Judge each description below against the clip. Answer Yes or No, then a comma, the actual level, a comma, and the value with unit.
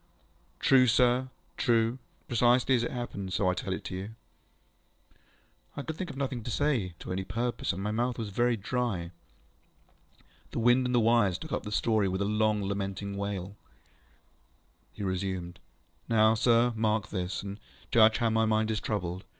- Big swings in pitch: No, average, 3.6 semitones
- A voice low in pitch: Yes, low, 110 Hz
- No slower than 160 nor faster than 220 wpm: Yes, average, 170 wpm